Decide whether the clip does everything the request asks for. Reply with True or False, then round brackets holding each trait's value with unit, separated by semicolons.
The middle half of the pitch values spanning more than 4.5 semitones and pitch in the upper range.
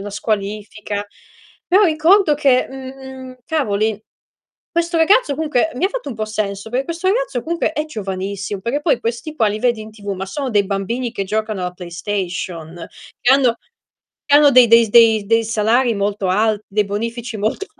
True (5.2 semitones; 230 Hz)